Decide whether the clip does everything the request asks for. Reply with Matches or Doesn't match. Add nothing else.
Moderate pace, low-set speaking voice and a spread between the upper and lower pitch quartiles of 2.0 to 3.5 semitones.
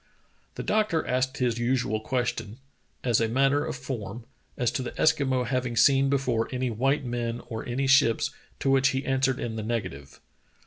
Matches